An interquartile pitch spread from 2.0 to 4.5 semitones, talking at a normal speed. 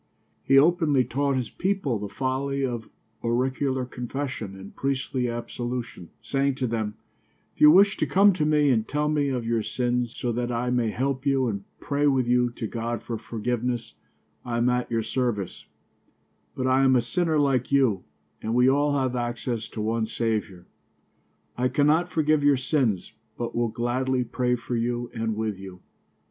Yes: average, 2.9 semitones; average, 175 wpm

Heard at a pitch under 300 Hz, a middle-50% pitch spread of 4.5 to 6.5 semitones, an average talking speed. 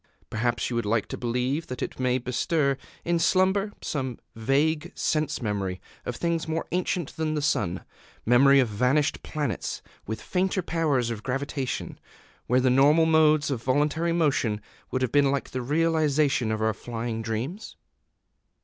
Yes: low, 135 Hz; average, 4.8 semitones; average, 160 wpm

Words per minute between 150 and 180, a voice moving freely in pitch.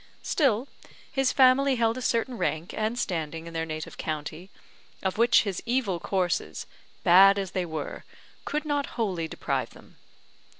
Yes: average, 155 wpm; wide, 6.6 semitones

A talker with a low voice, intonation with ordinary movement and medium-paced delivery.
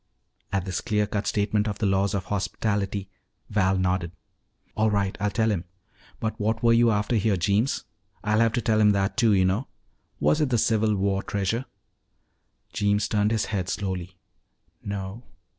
No: low, 105 Hz; narrow, 2.2 semitones; average, 175 wpm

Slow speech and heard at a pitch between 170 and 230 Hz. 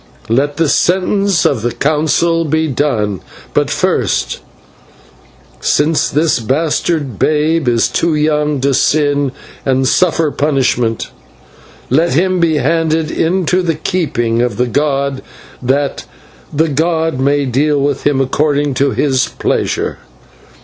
No: slow, 125 wpm; medium, 145 Hz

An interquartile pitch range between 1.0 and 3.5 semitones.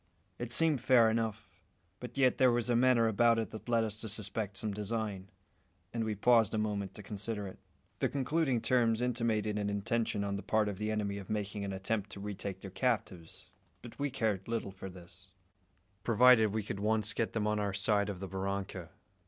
Yes: narrow, 2.6 semitones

